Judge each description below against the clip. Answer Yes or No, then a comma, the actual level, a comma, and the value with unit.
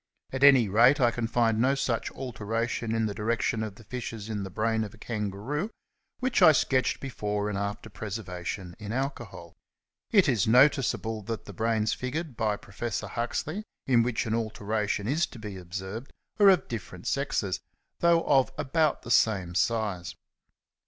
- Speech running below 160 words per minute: No, average, 165 wpm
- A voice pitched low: Yes, low, 115 Hz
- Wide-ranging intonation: No, average, 3.8 semitones